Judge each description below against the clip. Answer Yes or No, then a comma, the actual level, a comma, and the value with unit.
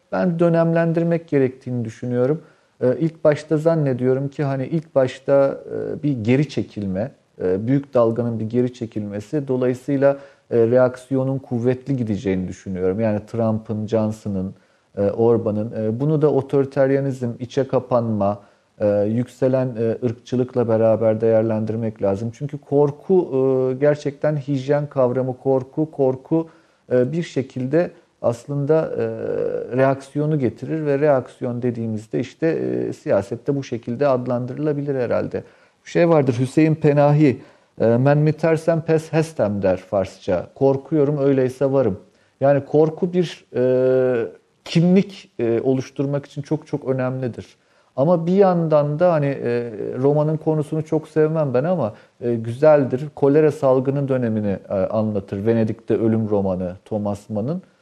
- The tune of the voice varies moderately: Yes, average, 4.6 semitones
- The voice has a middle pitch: No, low, 130 Hz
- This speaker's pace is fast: No, average, 115 wpm